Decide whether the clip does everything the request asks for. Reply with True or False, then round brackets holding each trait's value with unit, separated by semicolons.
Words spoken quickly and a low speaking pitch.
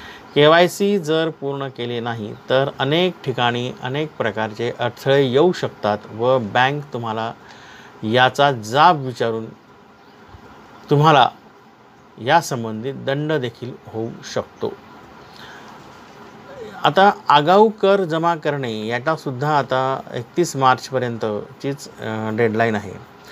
False (95 wpm; 130 Hz)